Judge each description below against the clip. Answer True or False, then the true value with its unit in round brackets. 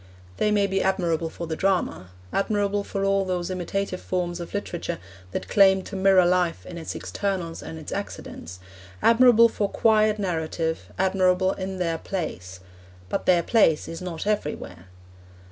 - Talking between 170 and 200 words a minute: False (155 wpm)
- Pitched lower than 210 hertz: True (185 Hz)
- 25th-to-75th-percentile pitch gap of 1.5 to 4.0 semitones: True (2.9 semitones)